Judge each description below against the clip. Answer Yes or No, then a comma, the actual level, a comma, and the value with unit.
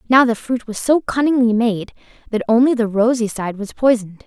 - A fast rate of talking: No, average, 195 wpm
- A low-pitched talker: No, high, 235 Hz